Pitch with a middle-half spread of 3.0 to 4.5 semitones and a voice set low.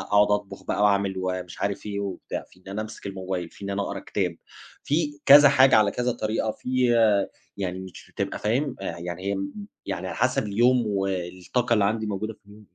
Yes: average, 3.4 semitones; low, 100 Hz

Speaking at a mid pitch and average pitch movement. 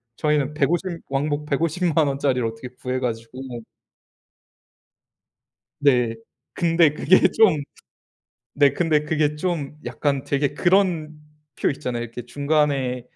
Yes: medium, 145 Hz; average, 3.5 semitones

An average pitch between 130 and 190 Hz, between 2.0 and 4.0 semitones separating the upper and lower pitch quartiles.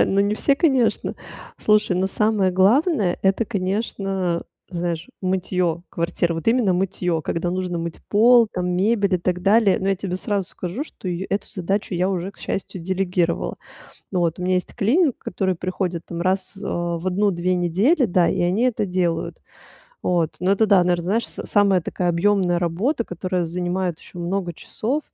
Yes: medium, 185 Hz; narrow, 2.6 semitones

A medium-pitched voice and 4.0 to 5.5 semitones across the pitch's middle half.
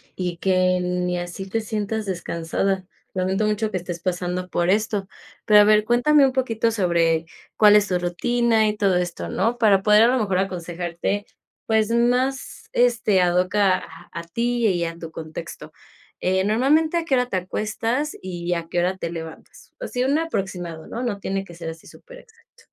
No: high, 195 Hz; average, 4.5 semitones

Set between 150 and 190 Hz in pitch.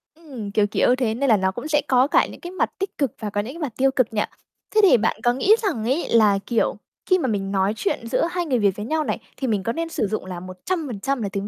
No: high, 240 Hz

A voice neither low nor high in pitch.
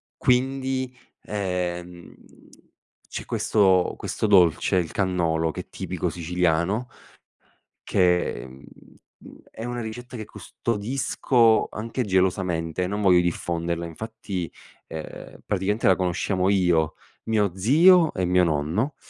No: very low, 95 Hz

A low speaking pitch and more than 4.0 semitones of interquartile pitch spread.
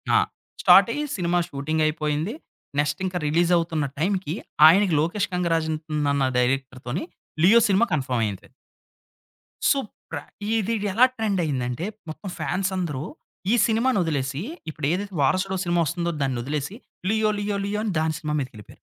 No: medium, 170 Hz; wide, 5.4 semitones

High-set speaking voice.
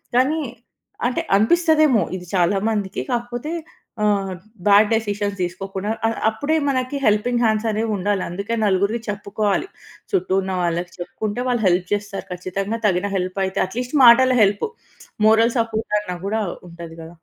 Yes: high, 210 Hz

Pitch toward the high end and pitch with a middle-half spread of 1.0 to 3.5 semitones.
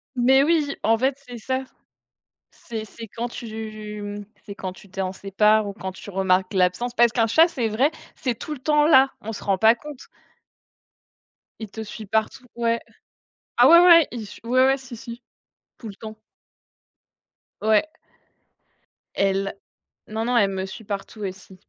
No: high, 220 Hz; average, 3.9 semitones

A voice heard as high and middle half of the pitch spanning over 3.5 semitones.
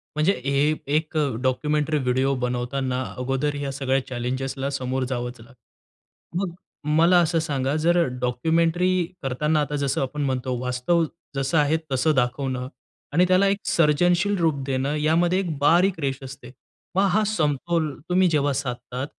No: medium, 145 Hz; average, 4.1 semitones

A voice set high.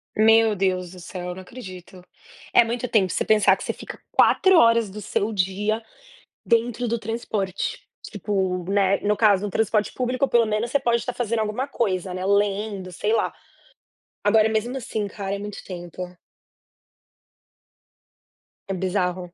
Yes: high, 210 Hz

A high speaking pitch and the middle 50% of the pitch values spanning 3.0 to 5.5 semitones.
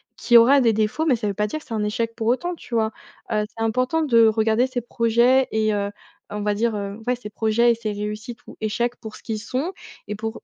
No: high, 225 Hz; narrow, 2.4 semitones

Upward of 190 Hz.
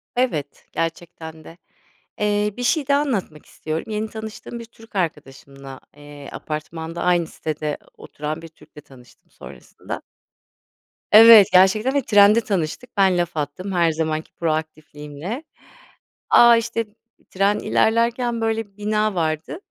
No: medium, 185 Hz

